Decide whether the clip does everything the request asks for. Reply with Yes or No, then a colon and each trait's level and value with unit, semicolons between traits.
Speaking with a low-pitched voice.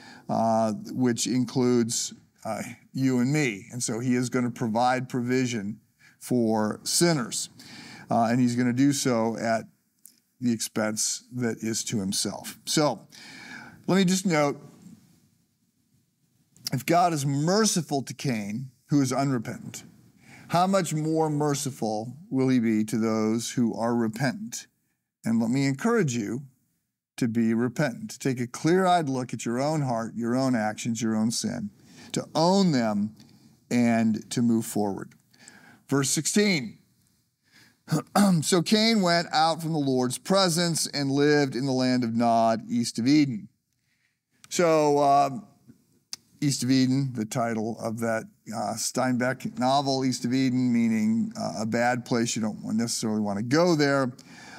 Yes: low, 130 Hz